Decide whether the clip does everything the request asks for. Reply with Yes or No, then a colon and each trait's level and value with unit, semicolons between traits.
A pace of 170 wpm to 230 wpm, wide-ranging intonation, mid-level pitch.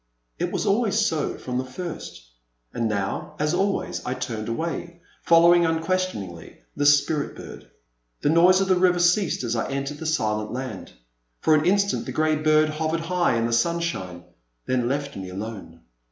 Yes: average, 180 wpm; wide, 6.6 semitones; medium, 155 Hz